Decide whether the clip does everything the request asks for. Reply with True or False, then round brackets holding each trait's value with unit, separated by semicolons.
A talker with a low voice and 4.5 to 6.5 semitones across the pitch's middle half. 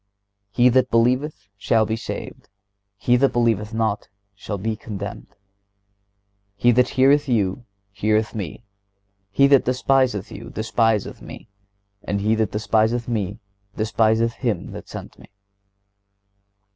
False (110 Hz; 2.6 semitones)